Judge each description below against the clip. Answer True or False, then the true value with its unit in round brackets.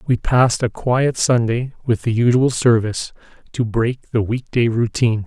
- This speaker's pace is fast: False (170 wpm)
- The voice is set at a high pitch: False (120 Hz)